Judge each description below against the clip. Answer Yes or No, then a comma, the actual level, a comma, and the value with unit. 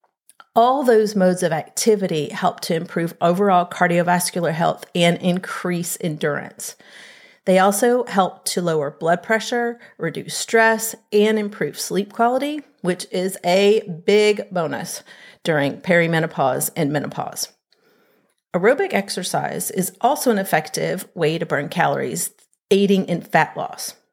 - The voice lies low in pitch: No, medium, 185 Hz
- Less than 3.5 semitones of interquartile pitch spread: No, average, 4.6 semitones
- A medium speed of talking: No, slow, 125 wpm